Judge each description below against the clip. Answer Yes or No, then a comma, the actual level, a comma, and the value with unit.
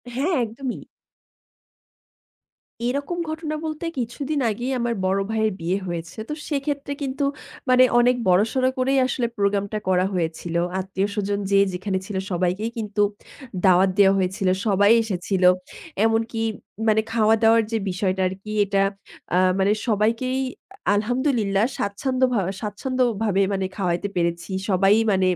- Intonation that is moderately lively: Yes, average, 4.5 semitones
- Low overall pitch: No, high, 210 Hz